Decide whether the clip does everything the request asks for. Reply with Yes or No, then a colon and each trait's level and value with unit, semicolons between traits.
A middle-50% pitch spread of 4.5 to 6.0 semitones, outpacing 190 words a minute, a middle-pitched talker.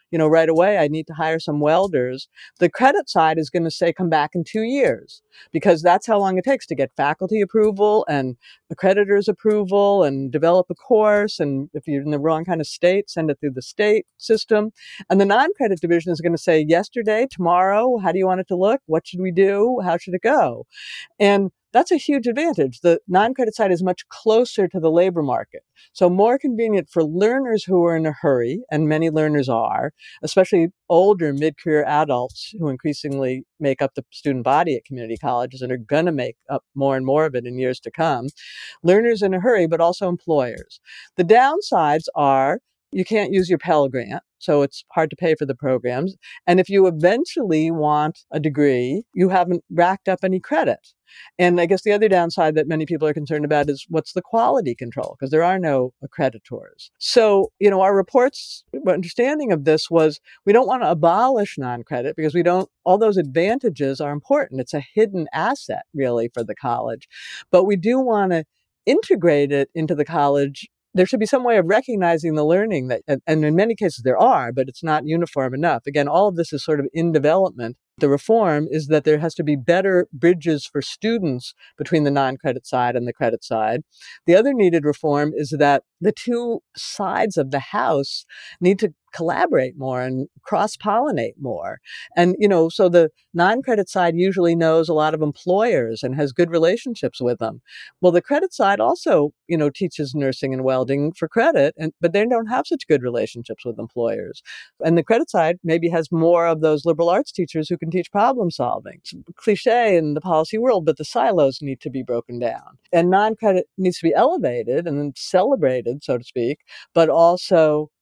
Yes: average, 5.0 semitones; average, 200 wpm; medium, 165 Hz